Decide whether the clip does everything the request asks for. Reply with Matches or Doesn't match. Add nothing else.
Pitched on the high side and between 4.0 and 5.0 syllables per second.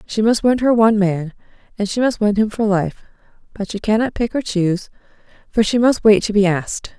Doesn't match